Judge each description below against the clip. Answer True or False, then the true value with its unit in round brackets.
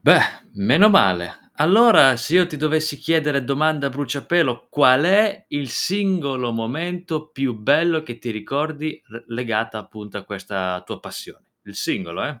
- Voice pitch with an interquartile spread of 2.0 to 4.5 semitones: False (5.5 semitones)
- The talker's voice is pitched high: False (140 Hz)